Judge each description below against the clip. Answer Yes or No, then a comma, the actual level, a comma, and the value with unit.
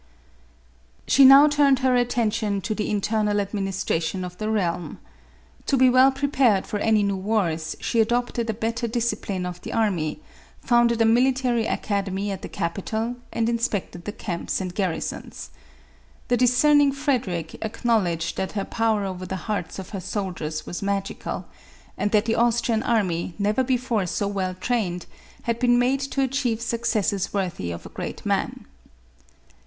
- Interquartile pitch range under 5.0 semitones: Yes, average, 4.0 semitones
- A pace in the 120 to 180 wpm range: Yes, average, 160 wpm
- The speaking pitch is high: Yes, high, 215 Hz